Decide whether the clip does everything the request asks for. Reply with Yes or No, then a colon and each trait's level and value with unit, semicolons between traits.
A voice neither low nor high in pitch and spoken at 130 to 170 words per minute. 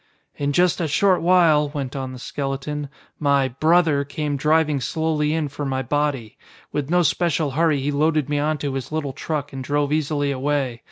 No: medium, 145 Hz; average, 180 wpm